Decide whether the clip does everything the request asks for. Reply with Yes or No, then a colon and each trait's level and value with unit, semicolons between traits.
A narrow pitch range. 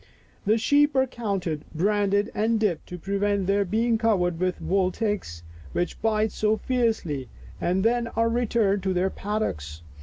No: average, 3.7 semitones